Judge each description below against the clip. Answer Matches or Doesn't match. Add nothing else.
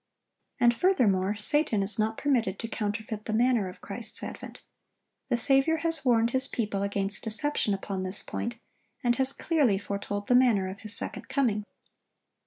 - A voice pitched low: Doesn't match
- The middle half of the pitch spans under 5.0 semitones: Matches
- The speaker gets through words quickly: Doesn't match